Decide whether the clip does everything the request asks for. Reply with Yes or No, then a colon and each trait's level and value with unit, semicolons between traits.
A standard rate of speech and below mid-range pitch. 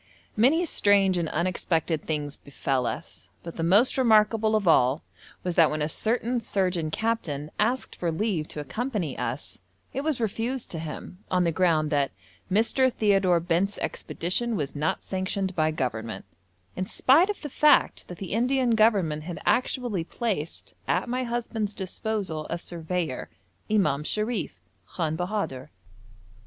No: average, 150 wpm; medium, 185 Hz